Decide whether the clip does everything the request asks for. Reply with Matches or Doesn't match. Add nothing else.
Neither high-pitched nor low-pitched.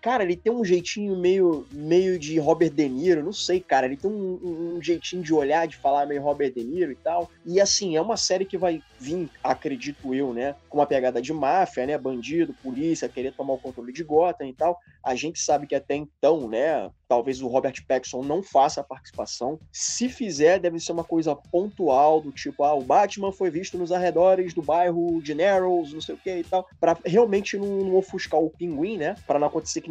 Matches